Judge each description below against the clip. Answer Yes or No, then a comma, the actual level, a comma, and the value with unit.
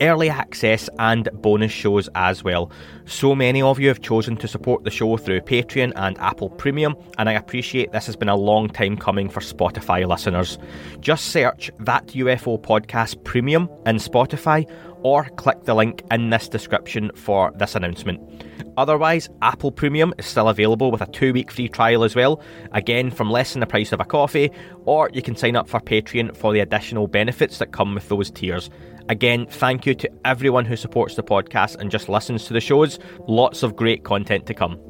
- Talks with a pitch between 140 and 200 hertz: No, low, 115 Hz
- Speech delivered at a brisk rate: No, average, 195 wpm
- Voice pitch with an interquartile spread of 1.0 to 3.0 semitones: No, average, 3.8 semitones